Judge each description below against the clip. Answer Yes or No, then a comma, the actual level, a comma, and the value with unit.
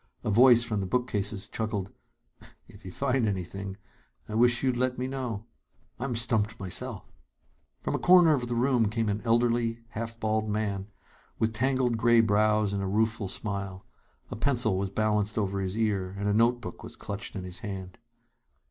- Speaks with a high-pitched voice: No, low, 110 Hz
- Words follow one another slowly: No, average, 175 wpm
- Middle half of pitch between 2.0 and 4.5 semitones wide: Yes, average, 3.1 semitones